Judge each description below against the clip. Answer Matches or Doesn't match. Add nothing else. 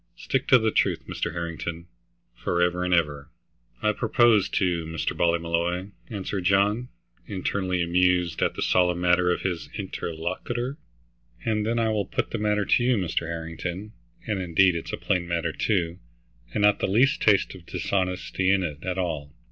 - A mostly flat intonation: Doesn't match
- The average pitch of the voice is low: Matches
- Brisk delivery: Doesn't match